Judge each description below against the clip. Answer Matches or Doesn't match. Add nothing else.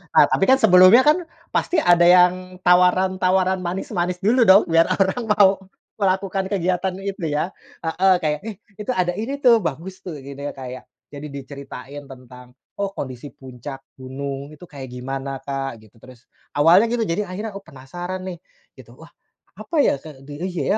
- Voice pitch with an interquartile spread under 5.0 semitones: Doesn't match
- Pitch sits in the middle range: Matches